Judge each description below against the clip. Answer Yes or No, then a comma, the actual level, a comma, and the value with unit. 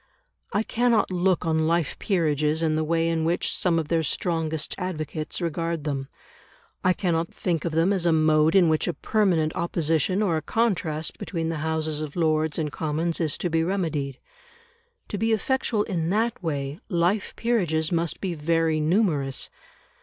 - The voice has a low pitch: No, medium, 165 Hz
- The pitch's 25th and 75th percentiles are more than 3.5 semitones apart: No, average, 2.7 semitones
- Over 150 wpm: Yes, average, 170 wpm